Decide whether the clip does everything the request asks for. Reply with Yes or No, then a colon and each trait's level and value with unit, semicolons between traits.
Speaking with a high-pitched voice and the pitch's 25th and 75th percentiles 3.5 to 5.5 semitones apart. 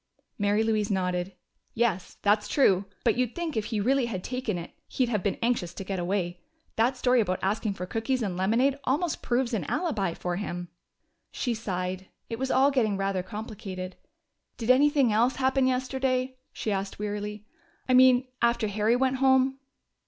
Yes: high, 220 Hz; average, 4.8 semitones